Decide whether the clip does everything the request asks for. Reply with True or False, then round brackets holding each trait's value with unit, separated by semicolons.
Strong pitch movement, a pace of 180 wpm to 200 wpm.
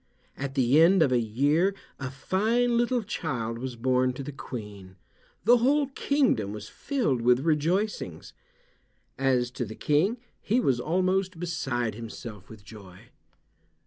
False (8.2 semitones; 145 wpm)